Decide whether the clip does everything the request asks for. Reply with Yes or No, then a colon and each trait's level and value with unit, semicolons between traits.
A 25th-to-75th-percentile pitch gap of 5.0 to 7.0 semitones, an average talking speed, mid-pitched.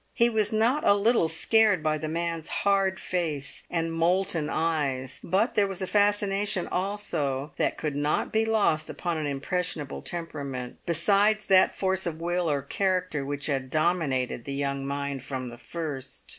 Yes: wide, 5.4 semitones; average, 165 wpm; medium, 165 Hz